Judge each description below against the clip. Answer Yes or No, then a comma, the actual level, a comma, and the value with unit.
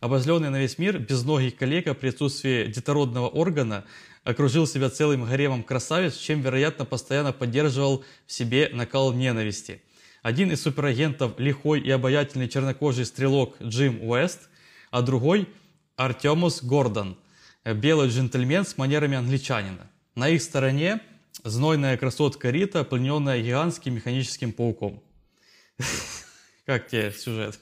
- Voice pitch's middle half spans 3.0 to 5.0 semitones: Yes, average, 3.3 semitones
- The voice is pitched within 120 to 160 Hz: Yes, low, 135 Hz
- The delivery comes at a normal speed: Yes, average, 120 wpm